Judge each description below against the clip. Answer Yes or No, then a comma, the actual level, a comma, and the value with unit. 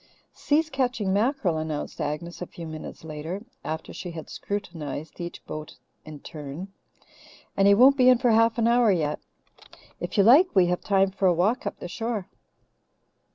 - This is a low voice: No, high, 190 Hz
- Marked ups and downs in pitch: Yes, wide, 6.4 semitones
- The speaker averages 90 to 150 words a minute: No, average, 170 wpm